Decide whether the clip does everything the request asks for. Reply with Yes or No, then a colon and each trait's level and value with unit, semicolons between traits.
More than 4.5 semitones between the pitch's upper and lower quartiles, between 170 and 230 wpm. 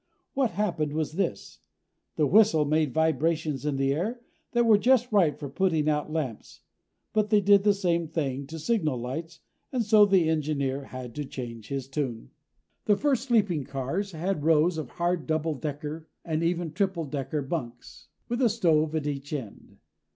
Yes: average, 5.2 semitones; average, 175 wpm